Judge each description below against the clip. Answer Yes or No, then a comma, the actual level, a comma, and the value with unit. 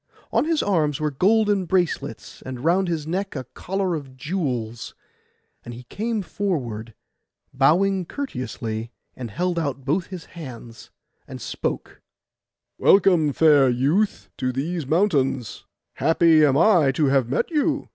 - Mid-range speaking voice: Yes, medium, 155 Hz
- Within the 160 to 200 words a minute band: No, slow, 135 wpm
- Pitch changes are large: Yes, wide, 6.2 semitones